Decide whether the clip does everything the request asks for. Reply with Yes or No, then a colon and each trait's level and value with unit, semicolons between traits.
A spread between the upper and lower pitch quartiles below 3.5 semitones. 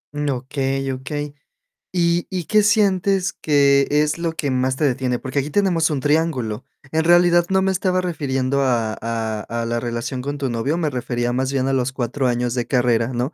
No: average, 4.7 semitones